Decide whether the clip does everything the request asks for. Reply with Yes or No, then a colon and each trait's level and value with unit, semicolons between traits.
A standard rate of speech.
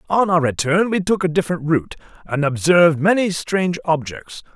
Yes: average, 170 wpm